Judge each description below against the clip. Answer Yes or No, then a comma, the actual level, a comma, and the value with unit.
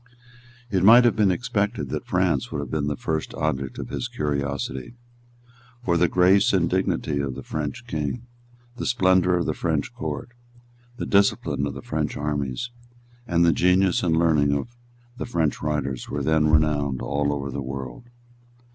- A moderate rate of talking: Yes, average, 170 wpm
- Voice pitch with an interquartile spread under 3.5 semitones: No, average, 4.6 semitones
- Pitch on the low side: Yes, very low, 80 Hz